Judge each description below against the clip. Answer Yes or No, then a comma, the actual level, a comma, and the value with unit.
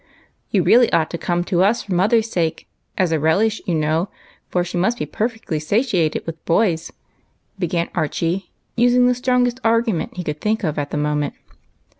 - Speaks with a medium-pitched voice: Yes, medium, 180 Hz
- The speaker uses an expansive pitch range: Yes, wide, 5.8 semitones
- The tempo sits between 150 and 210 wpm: Yes, average, 190 wpm